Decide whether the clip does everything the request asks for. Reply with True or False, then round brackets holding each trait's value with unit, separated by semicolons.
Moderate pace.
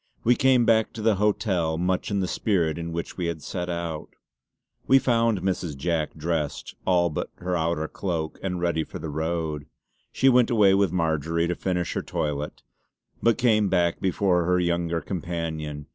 True (175 wpm)